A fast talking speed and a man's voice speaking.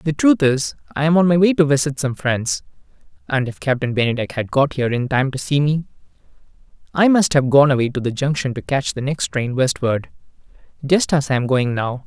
Yes: fast, 220 wpm; male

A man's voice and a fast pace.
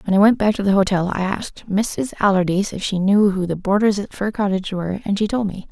No: female; fast, 260 wpm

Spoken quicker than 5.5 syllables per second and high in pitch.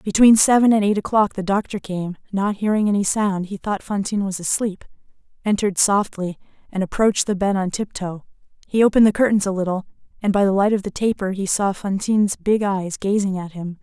Yes: 5.8 syllables/s; high, 200 Hz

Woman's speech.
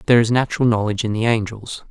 No: male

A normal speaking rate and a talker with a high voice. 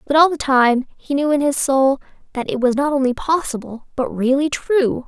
No: fast, 215 wpm; very high, 275 Hz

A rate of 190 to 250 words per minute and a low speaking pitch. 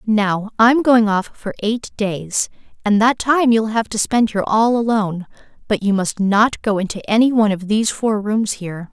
No: average, 200 wpm; high, 215 Hz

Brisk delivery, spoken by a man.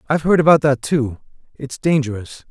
No: average, 170 wpm; male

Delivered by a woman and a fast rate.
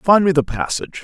No: male; fast, 235 wpm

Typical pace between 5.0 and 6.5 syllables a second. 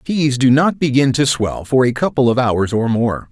No: 4.7 syllables/s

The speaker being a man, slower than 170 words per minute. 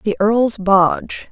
No: female; slow, 135 wpm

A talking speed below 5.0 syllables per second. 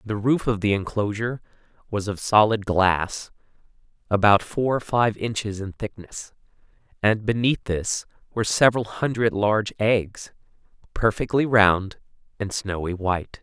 Yes: 4.6 syllables/s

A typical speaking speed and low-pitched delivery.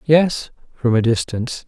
Yes: average, 145 wpm; low, 130 Hz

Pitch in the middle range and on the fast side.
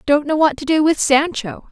No: very high, 290 Hz; fast, 245 wpm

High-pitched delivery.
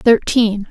Yes: high, 220 Hz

